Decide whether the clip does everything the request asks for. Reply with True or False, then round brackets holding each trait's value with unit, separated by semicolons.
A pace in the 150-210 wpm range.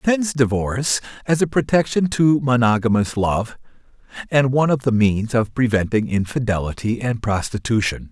False (135 wpm)